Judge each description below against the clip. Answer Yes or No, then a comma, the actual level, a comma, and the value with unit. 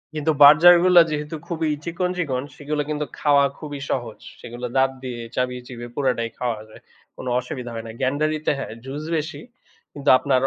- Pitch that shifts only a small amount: No, average, 3.4 semitones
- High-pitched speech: No, medium, 140 Hz